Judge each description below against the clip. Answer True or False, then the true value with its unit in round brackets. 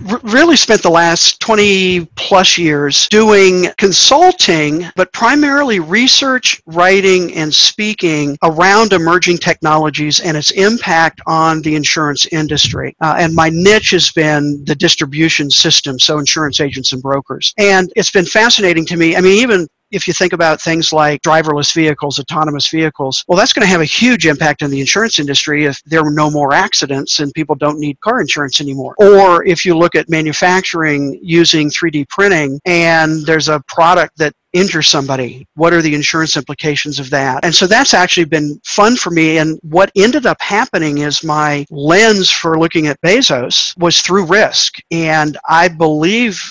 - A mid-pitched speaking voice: True (165 Hz)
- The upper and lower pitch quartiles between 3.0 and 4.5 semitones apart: True (3.6 semitones)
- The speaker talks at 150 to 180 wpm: True (170 wpm)